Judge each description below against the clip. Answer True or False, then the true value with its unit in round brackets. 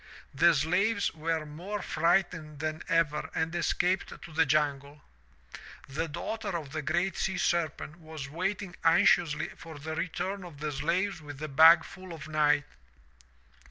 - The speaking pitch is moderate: True (160 Hz)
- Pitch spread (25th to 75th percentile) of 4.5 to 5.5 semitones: False (2.7 semitones)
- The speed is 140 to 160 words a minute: True (150 wpm)